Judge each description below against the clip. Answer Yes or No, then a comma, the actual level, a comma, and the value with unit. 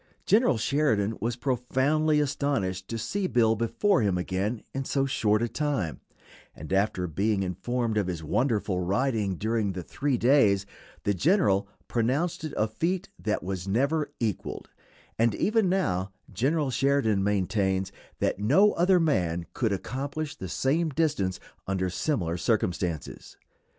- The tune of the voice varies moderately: No, wide, 6.7 semitones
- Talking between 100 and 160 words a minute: Yes, average, 140 wpm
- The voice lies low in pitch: Yes, low, 115 Hz